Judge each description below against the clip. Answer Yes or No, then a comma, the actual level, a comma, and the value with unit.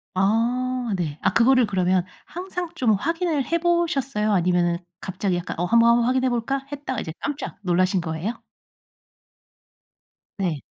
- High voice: Yes, high, 230 Hz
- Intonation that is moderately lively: No, wide, 6.5 semitones